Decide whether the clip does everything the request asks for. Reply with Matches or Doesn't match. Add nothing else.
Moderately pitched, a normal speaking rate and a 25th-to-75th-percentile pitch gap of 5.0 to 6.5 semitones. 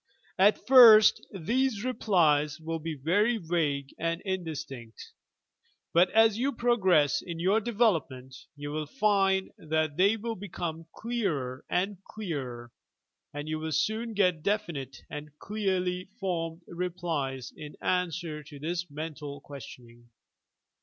Doesn't match